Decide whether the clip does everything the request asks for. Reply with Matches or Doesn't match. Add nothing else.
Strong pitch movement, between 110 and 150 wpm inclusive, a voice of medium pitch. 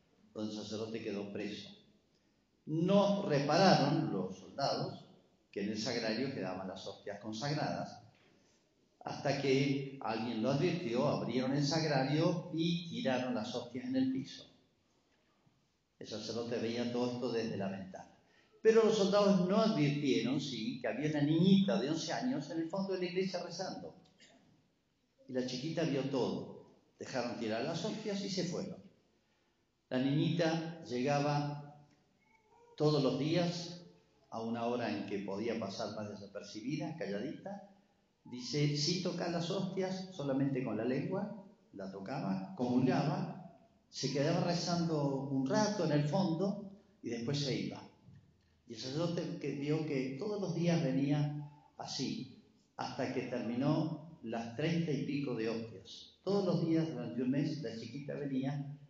Matches